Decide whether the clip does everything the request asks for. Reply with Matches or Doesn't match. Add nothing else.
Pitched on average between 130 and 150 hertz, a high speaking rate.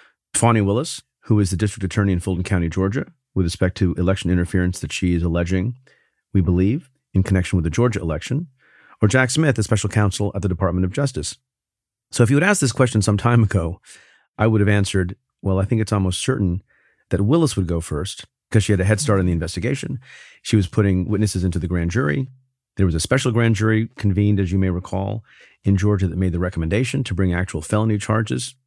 Doesn't match